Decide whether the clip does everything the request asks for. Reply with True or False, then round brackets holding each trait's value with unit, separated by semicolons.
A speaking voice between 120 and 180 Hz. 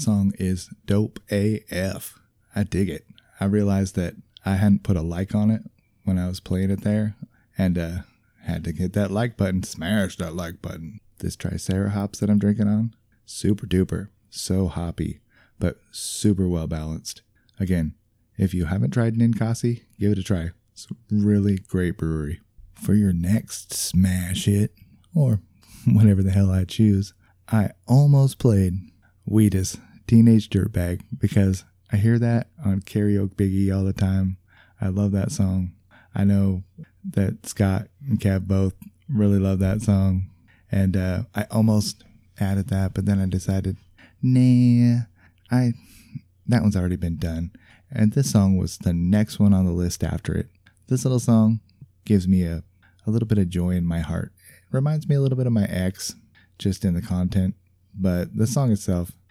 False (100 Hz)